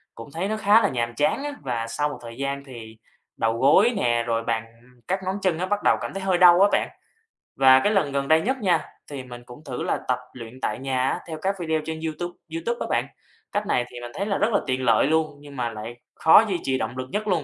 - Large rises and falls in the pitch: Yes, wide, 7.3 semitones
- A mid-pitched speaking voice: Yes, medium, 145 Hz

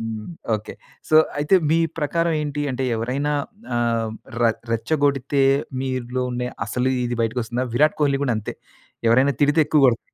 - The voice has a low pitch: Yes, low, 130 Hz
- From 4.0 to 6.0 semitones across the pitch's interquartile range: No, average, 3.6 semitones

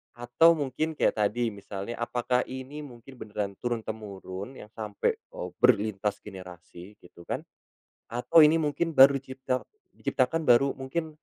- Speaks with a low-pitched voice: Yes, low, 120 Hz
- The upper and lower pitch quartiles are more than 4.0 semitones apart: Yes, average, 5.0 semitones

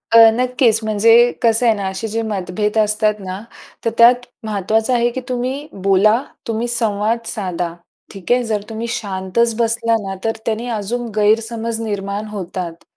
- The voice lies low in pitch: No, high, 220 Hz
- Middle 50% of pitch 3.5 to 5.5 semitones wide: No, narrow, 2.4 semitones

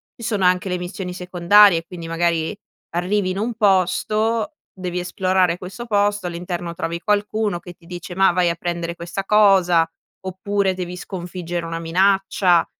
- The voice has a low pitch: No, medium, 180 Hz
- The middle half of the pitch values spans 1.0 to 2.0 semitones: No, narrow, 2.6 semitones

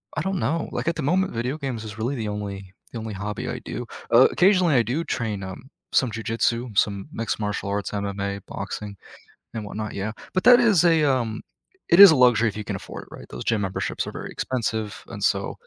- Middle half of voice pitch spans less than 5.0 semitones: No, wide, 5.5 semitones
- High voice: No, low, 115 Hz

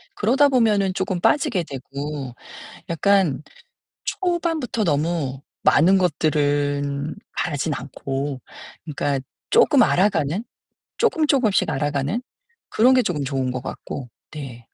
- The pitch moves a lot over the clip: Yes, wide, 6.8 semitones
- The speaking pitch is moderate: Yes, medium, 155 Hz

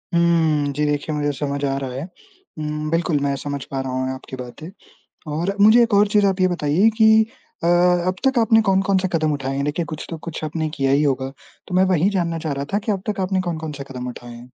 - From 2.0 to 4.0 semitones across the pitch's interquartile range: No, average, 4.8 semitones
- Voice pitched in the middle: Yes, medium, 155 Hz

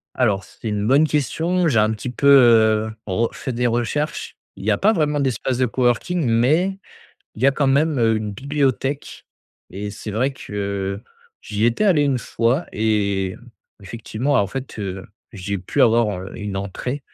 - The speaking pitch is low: Yes, low, 115 Hz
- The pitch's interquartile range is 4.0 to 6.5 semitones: Yes, average, 5.1 semitones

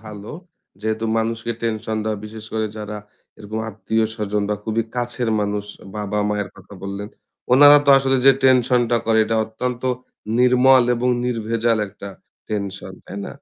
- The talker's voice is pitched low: Yes, low, 110 Hz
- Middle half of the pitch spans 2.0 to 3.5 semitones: Yes, narrow, 2.4 semitones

